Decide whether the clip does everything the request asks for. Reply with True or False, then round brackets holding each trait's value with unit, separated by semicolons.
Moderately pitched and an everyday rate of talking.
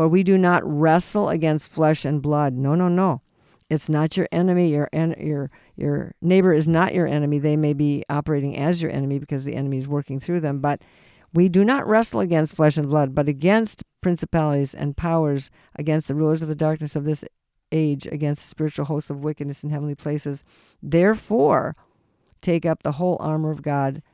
True (155 Hz; 195 wpm)